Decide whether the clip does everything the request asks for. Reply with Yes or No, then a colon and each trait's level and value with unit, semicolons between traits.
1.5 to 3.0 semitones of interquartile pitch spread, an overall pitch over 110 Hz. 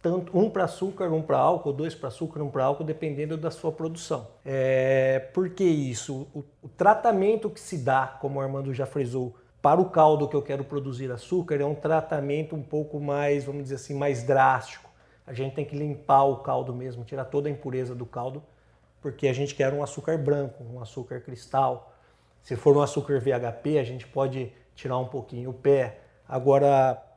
Yes: narrow, 2.5 semitones; medium, 140 Hz